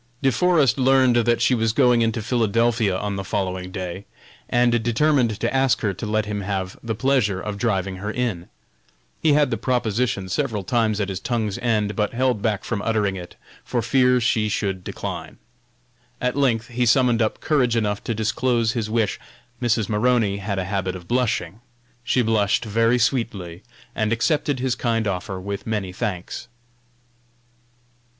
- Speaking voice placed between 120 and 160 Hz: No, low, 110 Hz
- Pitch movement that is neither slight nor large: Yes, average, 3.4 semitones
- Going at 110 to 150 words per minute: No, average, 170 wpm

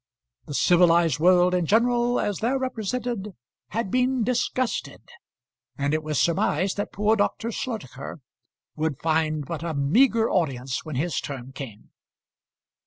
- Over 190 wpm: No, slow, 135 wpm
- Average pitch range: No, wide, 7.0 semitones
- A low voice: No, medium, 180 Hz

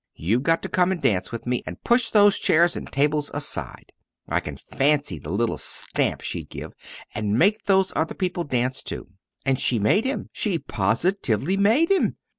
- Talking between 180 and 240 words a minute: Yes, average, 185 wpm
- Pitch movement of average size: No, wide, 8.5 semitones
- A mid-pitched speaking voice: Yes, medium, 150 Hz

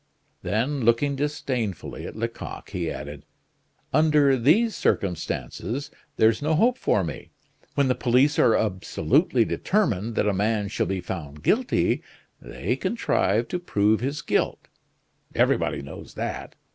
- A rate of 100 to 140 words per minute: Yes, slow, 135 wpm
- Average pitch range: No, wide, 6.5 semitones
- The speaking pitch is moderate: No, low, 115 Hz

